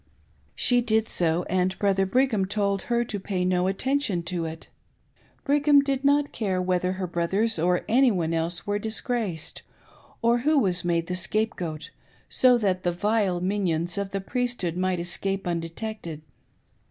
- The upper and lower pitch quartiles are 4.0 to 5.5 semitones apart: Yes, average, 4.4 semitones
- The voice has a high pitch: Yes, high, 195 Hz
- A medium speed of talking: Yes, average, 155 wpm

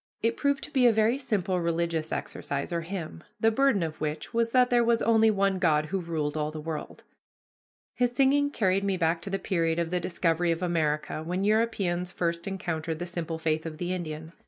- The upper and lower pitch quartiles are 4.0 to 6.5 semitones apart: Yes, average, 5.1 semitones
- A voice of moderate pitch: Yes, medium, 175 Hz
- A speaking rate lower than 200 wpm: No, fast, 205 wpm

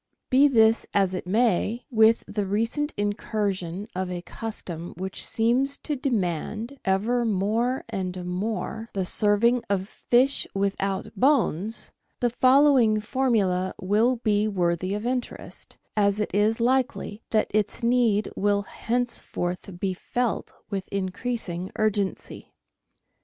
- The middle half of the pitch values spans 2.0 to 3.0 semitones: No, average, 3.8 semitones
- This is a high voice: Yes, high, 215 Hz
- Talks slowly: Yes, slow, 125 wpm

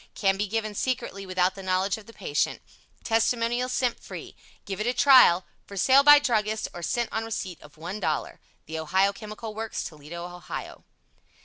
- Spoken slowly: No, average, 175 wpm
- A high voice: Yes, high, 205 Hz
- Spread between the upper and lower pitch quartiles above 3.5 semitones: Yes, average, 3.9 semitones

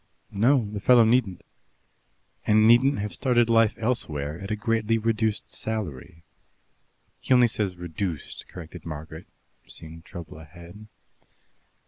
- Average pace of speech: No, slow, 125 wpm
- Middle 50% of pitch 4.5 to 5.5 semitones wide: Yes, average, 5.2 semitones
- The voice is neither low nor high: No, low, 105 Hz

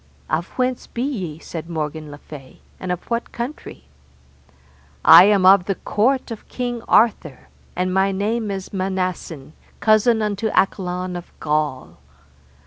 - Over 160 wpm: No, average, 140 wpm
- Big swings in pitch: No, average, 4.9 semitones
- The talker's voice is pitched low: No, high, 190 Hz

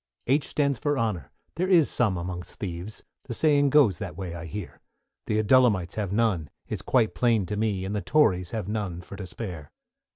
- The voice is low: Yes, low, 105 Hz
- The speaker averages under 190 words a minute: No, average, 195 wpm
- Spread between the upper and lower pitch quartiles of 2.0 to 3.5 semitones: No, average, 5.3 semitones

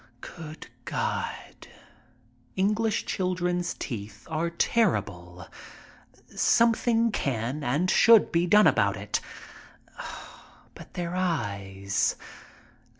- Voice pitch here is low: No, medium, 170 Hz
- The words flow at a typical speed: No, slow, 85 wpm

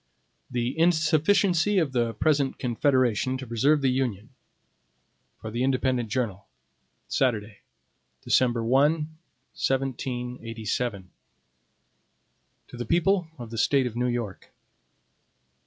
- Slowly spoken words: Yes, slow, 110 wpm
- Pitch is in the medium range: No, low, 125 Hz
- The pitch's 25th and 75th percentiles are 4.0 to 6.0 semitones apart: No, average, 3.2 semitones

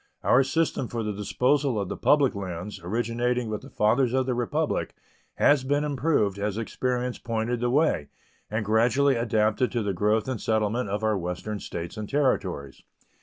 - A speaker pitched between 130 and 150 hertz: No, low, 115 Hz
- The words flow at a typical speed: Yes, average, 170 wpm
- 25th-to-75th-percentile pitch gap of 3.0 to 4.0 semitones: Yes, average, 3.5 semitones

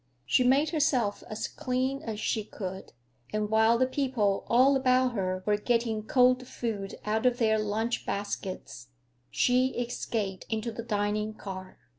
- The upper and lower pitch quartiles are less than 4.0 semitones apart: Yes, average, 3.4 semitones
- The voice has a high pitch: Yes, high, 225 Hz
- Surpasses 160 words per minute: No, average, 150 wpm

